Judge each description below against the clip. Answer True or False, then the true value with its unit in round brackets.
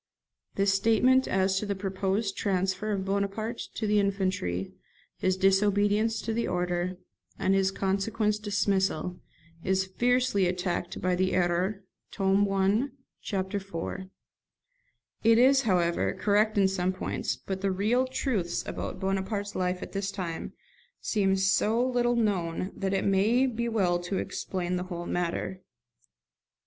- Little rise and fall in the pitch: True (2.2 semitones)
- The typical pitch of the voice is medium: False (195 Hz)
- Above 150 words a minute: False (140 wpm)